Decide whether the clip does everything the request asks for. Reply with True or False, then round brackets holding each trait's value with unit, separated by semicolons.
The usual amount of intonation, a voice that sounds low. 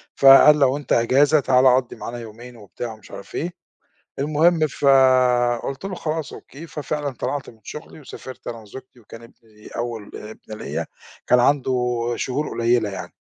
True (3.6 semitones; 125 Hz)